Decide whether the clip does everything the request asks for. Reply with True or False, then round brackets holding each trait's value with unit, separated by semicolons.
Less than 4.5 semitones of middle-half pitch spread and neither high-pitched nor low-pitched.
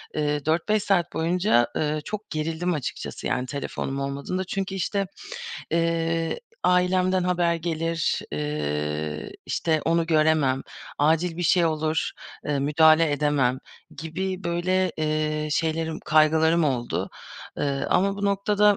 True (3.2 semitones; 160 Hz)